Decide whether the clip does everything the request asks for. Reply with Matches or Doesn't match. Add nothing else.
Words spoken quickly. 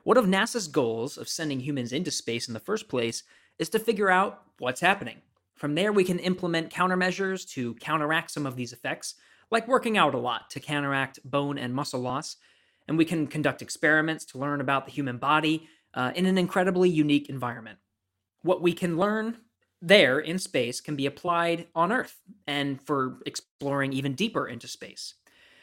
Doesn't match